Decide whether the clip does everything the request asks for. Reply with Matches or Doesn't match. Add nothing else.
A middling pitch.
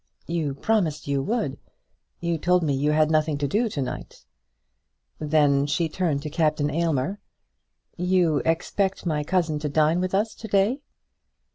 Matches